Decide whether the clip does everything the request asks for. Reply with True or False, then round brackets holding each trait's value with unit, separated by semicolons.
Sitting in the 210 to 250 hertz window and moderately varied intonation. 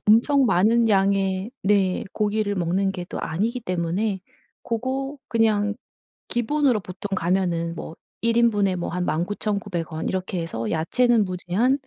False (200 Hz; 4.0 semitones)